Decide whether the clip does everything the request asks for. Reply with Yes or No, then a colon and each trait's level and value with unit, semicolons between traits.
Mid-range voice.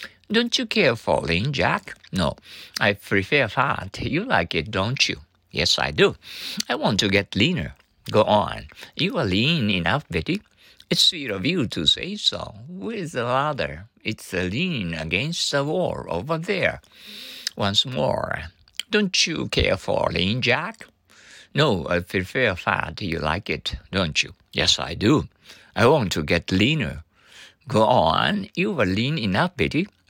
No: low, 105 Hz